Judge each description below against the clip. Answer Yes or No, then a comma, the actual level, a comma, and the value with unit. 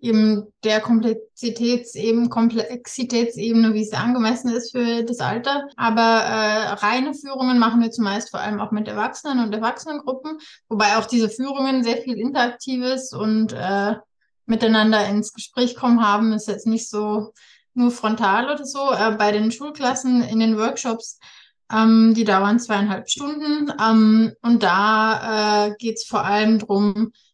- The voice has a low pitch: No, high, 225 Hz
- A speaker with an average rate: Yes, average, 150 wpm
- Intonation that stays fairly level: Yes, narrow, 2.2 semitones